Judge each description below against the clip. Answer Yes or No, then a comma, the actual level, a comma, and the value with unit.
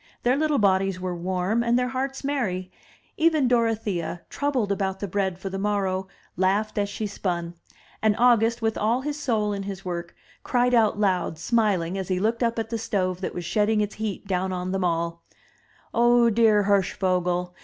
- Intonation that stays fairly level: No, average, 3.9 semitones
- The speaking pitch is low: No, high, 205 Hz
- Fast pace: No, average, 185 wpm